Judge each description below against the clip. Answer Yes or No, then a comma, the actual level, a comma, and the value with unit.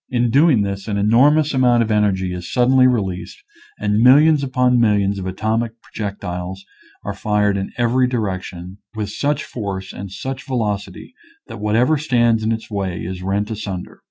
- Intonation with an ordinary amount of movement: Yes, average, 4.2 semitones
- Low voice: Yes, low, 105 Hz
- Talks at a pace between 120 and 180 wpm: Yes, average, 170 wpm